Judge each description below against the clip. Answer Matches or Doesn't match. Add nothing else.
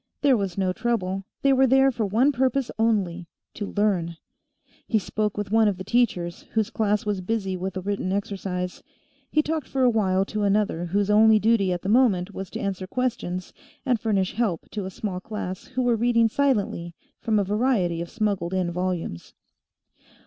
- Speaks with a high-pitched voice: Matches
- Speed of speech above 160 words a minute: Matches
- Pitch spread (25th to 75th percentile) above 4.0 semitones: Doesn't match